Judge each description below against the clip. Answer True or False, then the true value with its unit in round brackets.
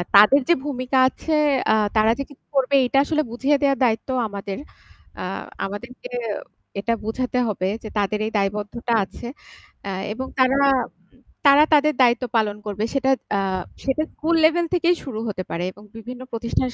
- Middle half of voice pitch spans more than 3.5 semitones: True (4.7 semitones)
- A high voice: True (250 Hz)